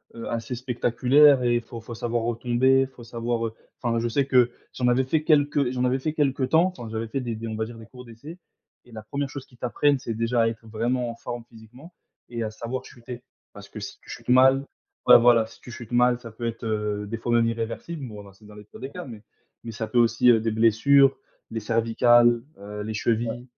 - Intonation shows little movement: Yes, narrow, 2.2 semitones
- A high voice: No, low, 120 Hz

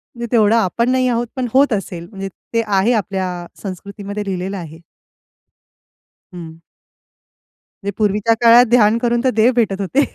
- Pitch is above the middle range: Yes, high, 210 Hz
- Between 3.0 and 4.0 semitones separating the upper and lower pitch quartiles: Yes, average, 3.7 semitones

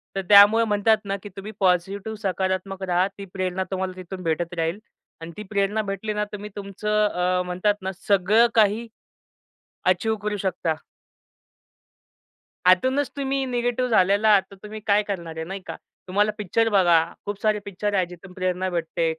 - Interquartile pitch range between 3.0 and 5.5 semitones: No, narrow, 2.4 semitones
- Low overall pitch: No, high, 200 Hz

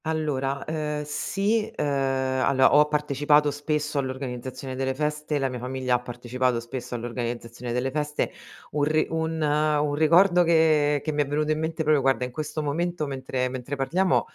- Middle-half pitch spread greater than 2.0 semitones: Yes, average, 2.7 semitones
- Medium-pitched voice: Yes, medium, 145 Hz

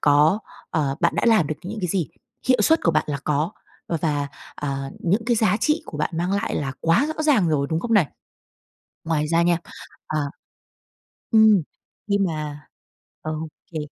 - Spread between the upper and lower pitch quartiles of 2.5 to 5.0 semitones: No, wide, 5.5 semitones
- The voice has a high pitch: No, medium, 165 Hz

